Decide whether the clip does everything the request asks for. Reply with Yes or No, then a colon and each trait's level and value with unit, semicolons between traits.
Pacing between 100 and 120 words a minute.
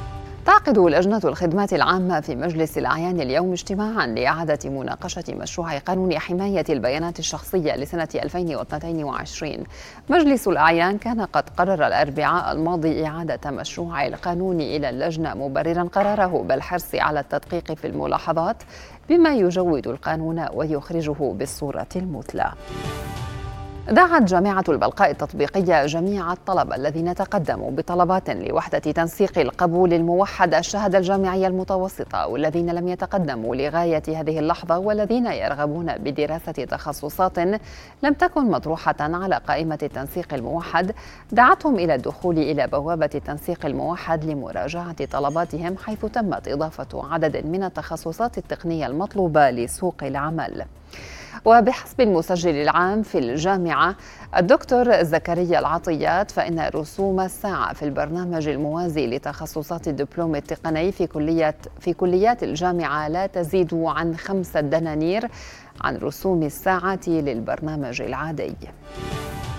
Yes: average, 110 wpm